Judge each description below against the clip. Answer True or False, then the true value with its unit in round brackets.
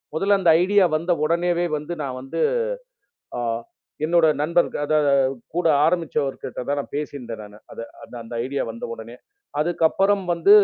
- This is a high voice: False (160 Hz)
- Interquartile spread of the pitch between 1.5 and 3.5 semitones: False (4.5 semitones)